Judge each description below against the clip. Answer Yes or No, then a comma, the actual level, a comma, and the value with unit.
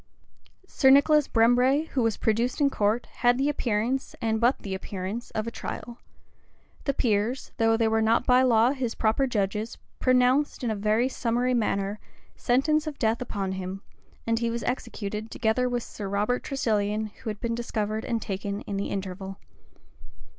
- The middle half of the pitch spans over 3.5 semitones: No, average, 3.0 semitones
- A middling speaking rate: Yes, average, 170 wpm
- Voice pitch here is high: Yes, high, 230 Hz